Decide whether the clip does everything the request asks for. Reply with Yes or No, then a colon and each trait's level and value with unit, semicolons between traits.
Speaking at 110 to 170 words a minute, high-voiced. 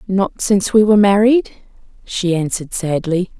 Yes: average, 140 wpm; high, 195 Hz